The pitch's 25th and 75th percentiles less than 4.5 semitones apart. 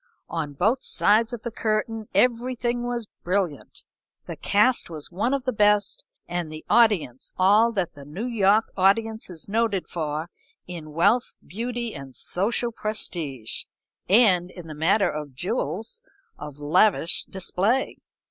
No: wide, 5.6 semitones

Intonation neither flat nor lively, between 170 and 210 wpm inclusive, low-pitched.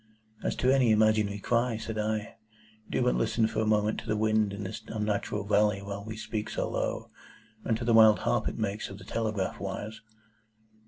No: narrow, 1.3 semitones; average, 200 wpm; low, 110 Hz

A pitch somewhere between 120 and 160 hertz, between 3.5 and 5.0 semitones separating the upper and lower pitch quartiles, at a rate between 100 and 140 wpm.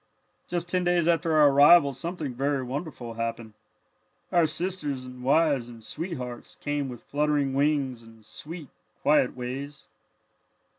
Yes: medium, 140 Hz; average, 4.2 semitones; slow, 135 wpm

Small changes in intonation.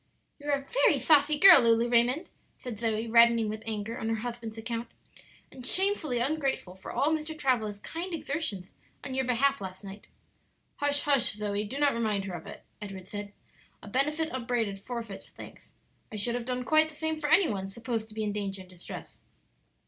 No: average, 5.3 semitones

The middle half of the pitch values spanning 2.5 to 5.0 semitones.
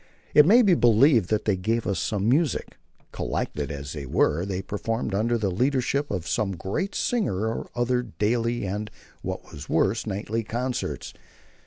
Yes: average, 4.3 semitones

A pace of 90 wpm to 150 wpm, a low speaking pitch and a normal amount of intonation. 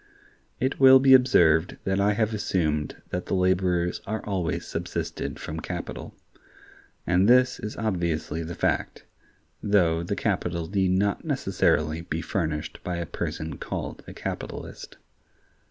Yes: average, 140 wpm; very low, 90 Hz; average, 3.8 semitones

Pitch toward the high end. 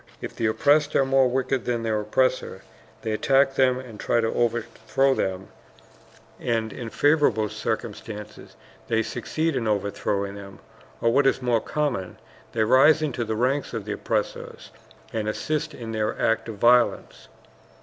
No: low, 115 Hz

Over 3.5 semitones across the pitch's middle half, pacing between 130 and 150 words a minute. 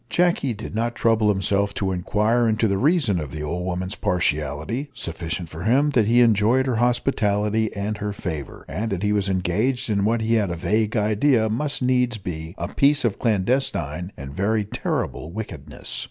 No: average, 4.3 semitones; average, 185 wpm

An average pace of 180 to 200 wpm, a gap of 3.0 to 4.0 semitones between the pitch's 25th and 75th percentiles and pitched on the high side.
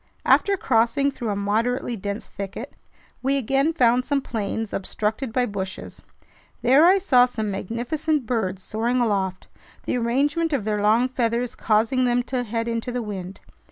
No: average, 160 wpm; average, 3.4 semitones; high, 235 Hz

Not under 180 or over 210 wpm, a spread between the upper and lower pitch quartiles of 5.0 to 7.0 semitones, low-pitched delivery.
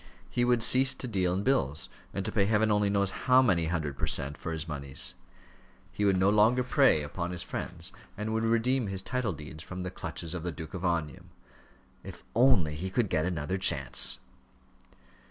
Yes: average, 195 wpm; wide, 5.5 semitones; very low, 95 Hz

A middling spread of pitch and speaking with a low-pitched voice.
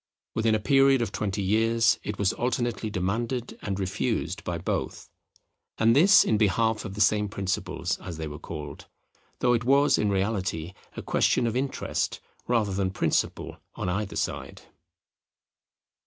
Yes: average, 3.6 semitones; low, 105 Hz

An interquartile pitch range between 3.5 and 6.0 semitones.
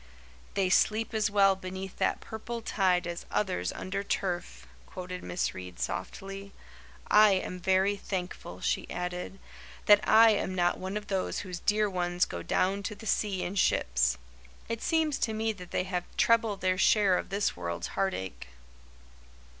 No: narrow, 2.6 semitones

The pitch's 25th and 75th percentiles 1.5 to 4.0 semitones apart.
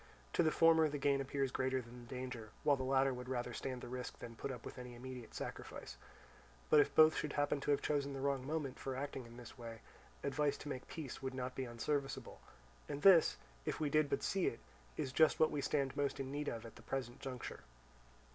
Yes: narrow, 2.5 semitones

